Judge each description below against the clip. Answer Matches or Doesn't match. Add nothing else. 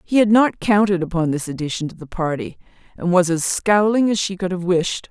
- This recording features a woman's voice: Matches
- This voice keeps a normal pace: Doesn't match